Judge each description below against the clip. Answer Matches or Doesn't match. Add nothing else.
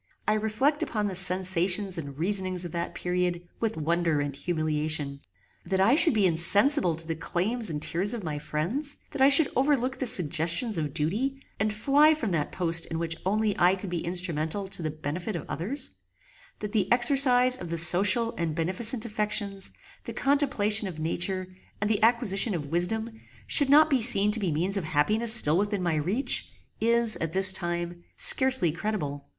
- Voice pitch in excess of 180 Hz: Matches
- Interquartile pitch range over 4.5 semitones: Matches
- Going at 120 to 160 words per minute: Doesn't match